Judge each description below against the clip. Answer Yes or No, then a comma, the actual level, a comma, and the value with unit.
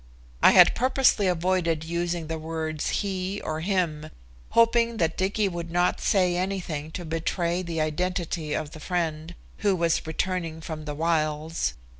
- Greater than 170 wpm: No, average, 150 wpm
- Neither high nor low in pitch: Yes, medium, 170 Hz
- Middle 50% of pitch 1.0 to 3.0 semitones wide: Yes, average, 2.7 semitones